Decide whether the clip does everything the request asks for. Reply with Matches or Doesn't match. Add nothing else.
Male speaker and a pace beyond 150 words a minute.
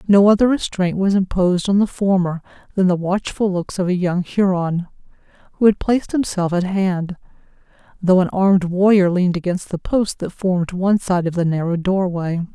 Doesn't match